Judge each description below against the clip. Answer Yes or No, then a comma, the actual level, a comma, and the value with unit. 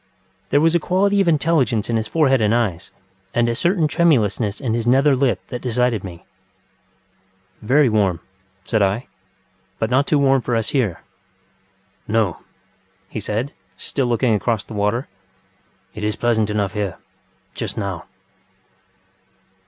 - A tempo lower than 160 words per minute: Yes, average, 145 wpm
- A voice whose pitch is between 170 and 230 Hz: No, low, 115 Hz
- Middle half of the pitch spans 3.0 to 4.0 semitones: No, average, 4.7 semitones